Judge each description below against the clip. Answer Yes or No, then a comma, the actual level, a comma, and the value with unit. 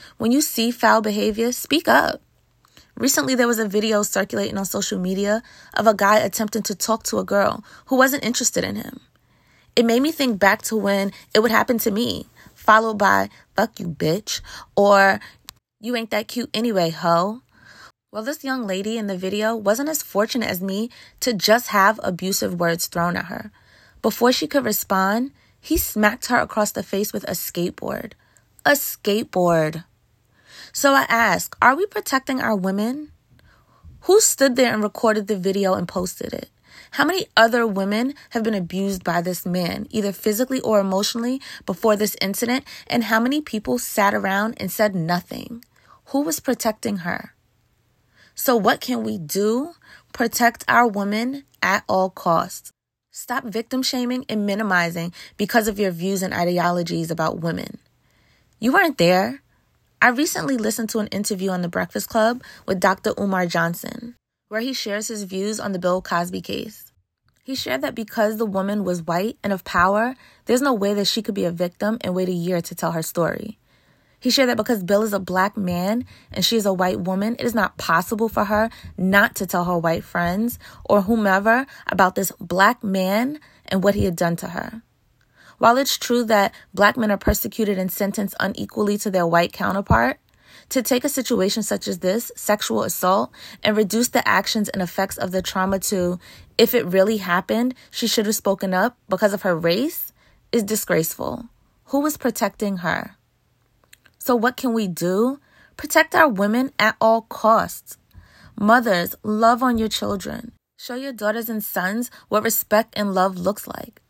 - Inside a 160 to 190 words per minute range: Yes, average, 175 wpm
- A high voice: Yes, high, 215 Hz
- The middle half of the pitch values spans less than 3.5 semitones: No, average, 4.0 semitones